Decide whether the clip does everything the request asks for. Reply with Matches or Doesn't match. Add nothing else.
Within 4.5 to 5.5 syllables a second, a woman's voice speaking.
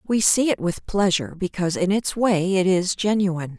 Matches